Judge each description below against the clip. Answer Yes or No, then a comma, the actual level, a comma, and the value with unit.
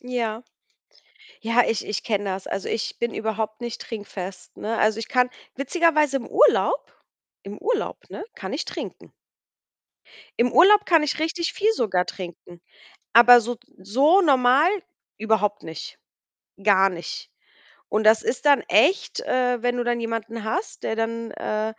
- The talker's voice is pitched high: Yes, high, 230 Hz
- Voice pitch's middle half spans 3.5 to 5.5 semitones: Yes, average, 4.2 semitones